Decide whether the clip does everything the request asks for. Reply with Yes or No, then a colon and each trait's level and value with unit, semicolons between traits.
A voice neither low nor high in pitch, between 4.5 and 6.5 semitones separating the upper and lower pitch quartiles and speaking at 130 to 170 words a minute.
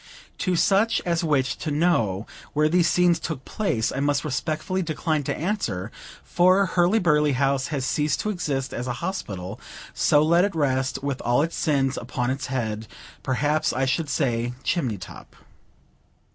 Yes: medium, 145 Hz; average, 4.8 semitones; average, 165 wpm